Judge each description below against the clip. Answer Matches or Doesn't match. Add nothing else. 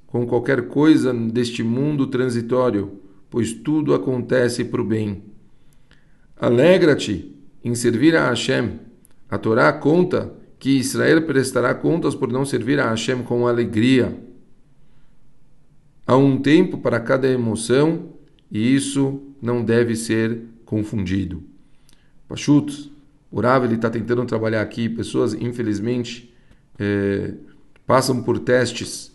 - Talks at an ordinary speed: Doesn't match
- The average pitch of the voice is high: Doesn't match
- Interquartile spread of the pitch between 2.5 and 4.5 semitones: Matches